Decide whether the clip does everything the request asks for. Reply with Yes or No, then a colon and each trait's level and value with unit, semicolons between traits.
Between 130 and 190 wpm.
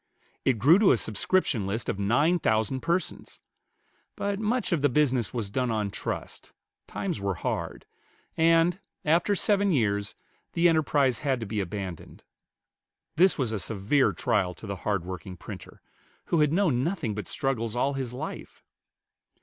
Yes: average, 160 wpm